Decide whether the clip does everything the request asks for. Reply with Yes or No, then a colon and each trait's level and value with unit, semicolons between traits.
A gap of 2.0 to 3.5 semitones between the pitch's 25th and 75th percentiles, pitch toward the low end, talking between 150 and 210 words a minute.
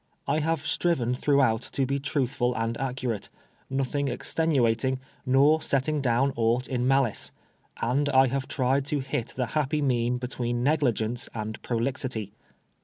No: average, 2.7 semitones; low, 130 Hz; average, 140 wpm